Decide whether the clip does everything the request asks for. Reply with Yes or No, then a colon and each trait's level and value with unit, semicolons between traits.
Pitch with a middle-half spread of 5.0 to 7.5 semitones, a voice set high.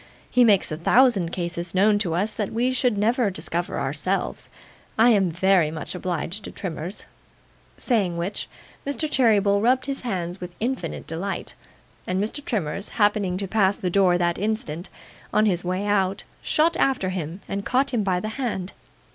No: average, 3.8 semitones; high, 195 Hz